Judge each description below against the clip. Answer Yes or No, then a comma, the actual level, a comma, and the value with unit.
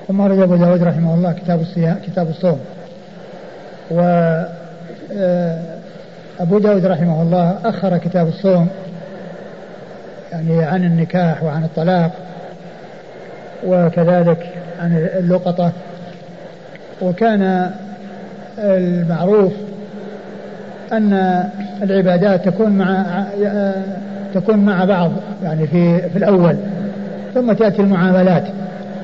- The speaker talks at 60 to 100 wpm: Yes, average, 85 wpm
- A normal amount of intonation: No, narrow, 1.8 semitones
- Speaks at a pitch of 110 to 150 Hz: No, medium, 185 Hz